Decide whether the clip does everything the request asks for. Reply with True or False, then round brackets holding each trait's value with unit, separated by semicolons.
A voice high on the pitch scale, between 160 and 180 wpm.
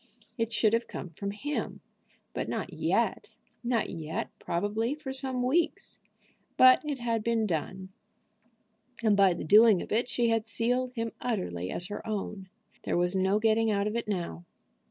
True (220 Hz; 170 wpm)